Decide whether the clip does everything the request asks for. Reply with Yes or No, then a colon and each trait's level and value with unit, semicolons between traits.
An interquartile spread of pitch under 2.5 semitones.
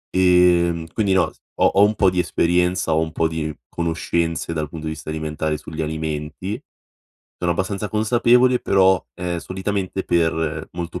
No: average, 2.9 semitones